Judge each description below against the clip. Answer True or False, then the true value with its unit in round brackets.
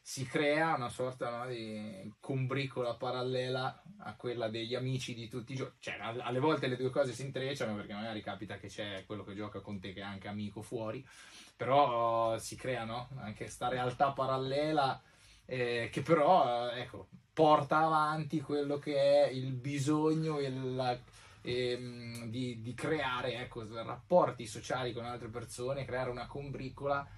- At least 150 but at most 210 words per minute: True (165 wpm)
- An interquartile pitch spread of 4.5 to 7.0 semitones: False (3.2 semitones)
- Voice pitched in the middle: False (125 Hz)